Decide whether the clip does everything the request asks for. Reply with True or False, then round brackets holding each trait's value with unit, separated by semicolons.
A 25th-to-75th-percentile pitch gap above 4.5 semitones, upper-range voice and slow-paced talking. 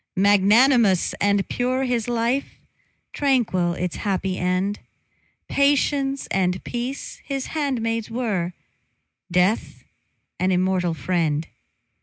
True (5.6 semitones; 205 Hz; 95 wpm)